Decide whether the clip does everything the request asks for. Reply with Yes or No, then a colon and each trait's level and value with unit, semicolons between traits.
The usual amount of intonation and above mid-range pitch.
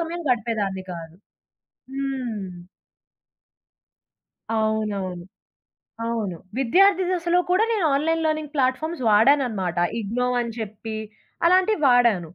No: wide, 7.3 semitones; high, 245 Hz